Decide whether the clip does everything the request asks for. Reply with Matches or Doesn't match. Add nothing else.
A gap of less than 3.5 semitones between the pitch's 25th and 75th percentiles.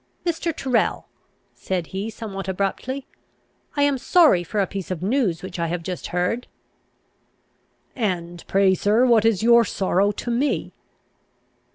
Doesn't match